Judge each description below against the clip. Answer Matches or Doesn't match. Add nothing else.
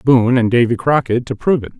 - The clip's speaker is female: Doesn't match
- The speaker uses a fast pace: Matches